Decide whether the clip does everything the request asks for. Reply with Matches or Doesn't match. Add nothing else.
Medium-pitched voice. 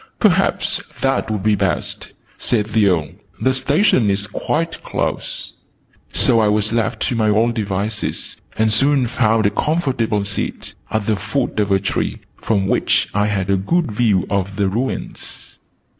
Doesn't match